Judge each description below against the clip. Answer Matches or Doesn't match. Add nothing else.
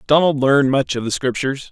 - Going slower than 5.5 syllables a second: Doesn't match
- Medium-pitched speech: Doesn't match